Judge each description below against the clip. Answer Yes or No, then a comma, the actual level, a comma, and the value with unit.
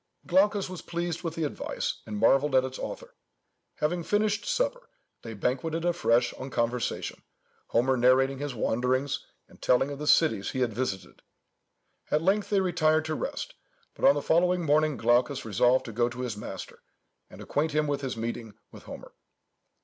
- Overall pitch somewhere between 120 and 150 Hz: Yes, medium, 140 Hz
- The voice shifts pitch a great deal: Yes, wide, 5.7 semitones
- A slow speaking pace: No, average, 170 wpm